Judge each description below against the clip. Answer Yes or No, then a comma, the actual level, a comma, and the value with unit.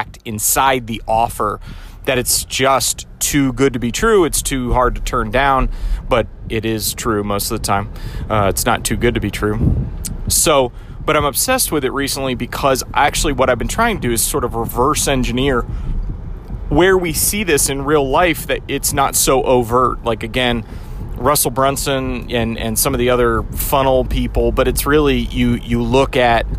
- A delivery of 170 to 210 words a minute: Yes, average, 190 wpm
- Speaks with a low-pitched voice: Yes, low, 125 Hz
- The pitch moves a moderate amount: Yes, average, 3.4 semitones